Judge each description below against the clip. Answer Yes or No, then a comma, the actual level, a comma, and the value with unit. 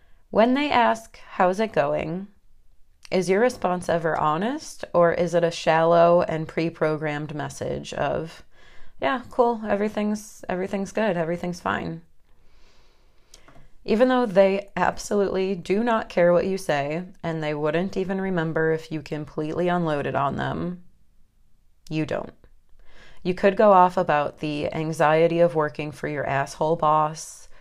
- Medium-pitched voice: Yes, medium, 170 Hz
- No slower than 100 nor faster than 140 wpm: Yes, slow, 135 wpm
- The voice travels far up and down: No, average, 4.1 semitones